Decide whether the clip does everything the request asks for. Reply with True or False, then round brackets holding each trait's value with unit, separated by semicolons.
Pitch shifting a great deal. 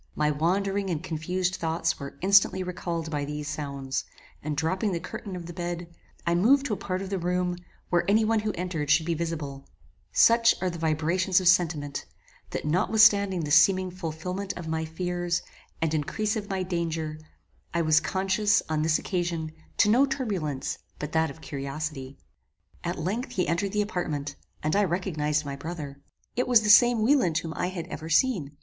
False (3.6 semitones)